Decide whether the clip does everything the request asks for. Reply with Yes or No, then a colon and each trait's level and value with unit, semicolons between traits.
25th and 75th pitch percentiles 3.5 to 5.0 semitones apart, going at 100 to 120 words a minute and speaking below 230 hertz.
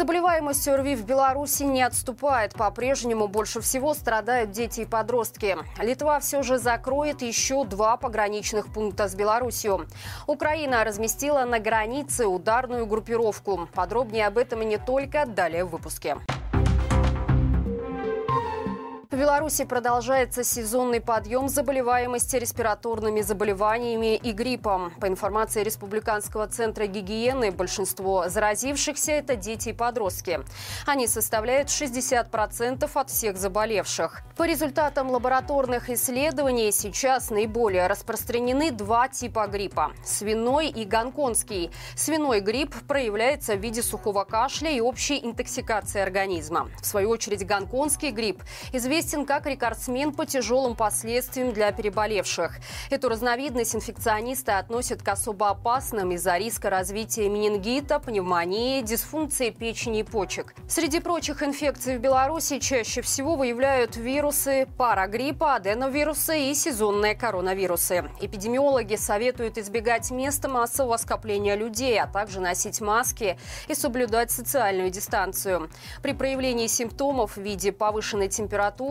No: average, 4.2 semitones; average, 115 wpm; high, 235 Hz